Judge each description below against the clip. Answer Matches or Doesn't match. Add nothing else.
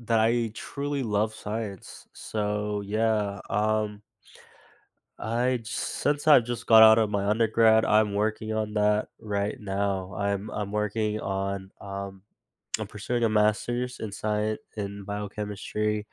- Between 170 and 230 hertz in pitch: Doesn't match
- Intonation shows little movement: Matches